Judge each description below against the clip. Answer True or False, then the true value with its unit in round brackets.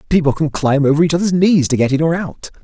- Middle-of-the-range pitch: True (155 Hz)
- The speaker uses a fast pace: True (275 wpm)